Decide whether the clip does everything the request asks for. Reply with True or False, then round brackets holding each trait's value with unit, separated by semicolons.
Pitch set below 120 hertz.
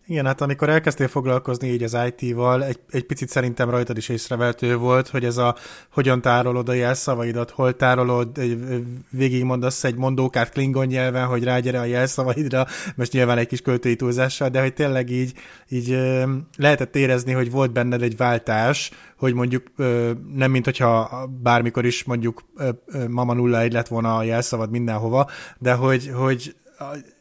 False (125 Hz)